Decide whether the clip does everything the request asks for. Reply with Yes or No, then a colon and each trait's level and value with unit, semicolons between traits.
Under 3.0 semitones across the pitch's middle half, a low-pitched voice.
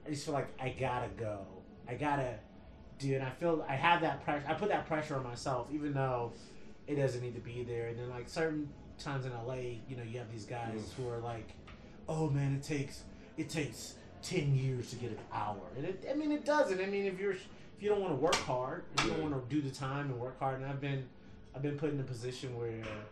No: average, 4.2 semitones; low, 130 Hz